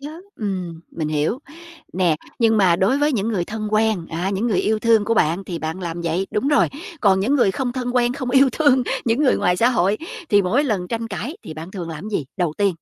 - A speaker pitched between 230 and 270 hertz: No, high, 205 Hz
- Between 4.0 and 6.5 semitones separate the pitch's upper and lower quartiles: Yes, average, 5.2 semitones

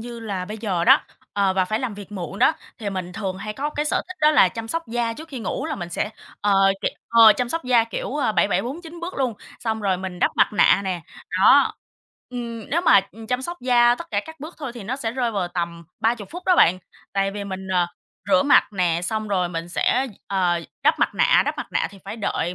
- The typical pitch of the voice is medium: No, high, 220 Hz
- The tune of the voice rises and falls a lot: No, average, 4.9 semitones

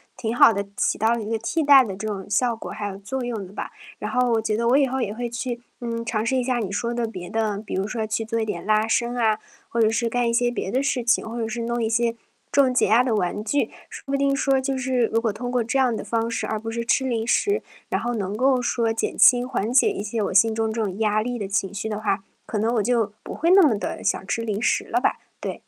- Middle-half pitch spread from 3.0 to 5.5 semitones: No, narrow, 2.4 semitones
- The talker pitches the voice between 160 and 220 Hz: No, high, 230 Hz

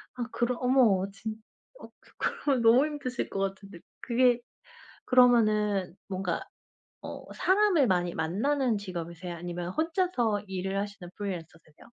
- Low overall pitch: No, high, 205 Hz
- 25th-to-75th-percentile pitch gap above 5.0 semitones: Yes, wide, 5.4 semitones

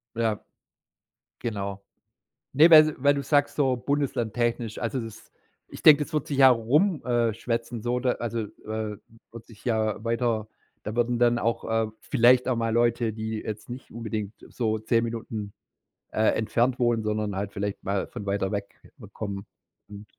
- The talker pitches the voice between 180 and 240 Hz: No, low, 115 Hz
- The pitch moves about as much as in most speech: No, narrow, 2.3 semitones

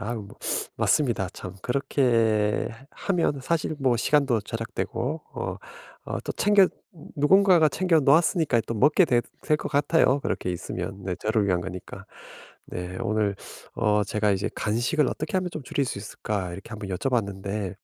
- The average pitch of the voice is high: No, low, 115 Hz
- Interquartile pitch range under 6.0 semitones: No, wide, 6.5 semitones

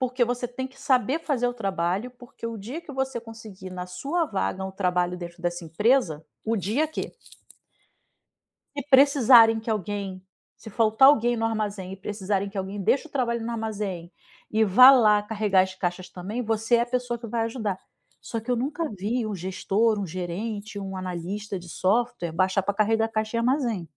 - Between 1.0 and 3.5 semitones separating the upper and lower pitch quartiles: No, average, 4.2 semitones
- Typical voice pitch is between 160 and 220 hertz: Yes, high, 215 Hz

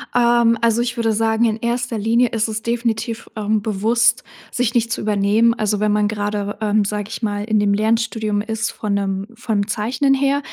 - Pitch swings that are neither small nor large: No, narrow, 2.0 semitones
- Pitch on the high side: Yes, high, 220 Hz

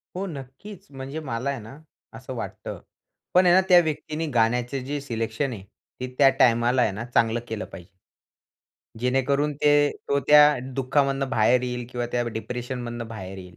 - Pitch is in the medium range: No, low, 125 Hz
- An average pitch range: Yes, average, 3.4 semitones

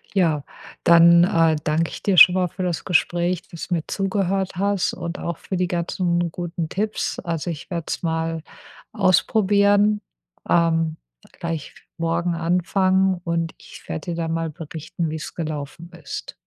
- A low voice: No, medium, 170 Hz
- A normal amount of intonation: No, narrow, 2.2 semitones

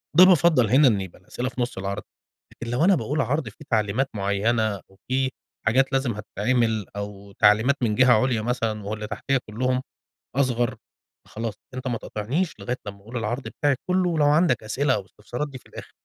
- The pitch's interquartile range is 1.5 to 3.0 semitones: No, average, 4.0 semitones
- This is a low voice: Yes, low, 120 Hz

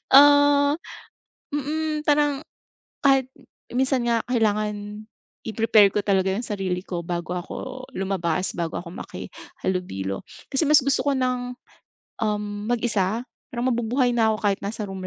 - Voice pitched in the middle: No, high, 225 Hz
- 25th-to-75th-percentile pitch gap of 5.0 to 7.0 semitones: Yes, wide, 5.4 semitones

